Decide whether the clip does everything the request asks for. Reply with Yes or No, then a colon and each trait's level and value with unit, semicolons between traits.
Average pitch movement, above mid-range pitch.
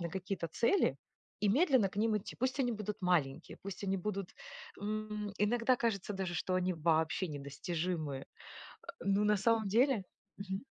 Yes: average, 3.4 semitones; high, 195 Hz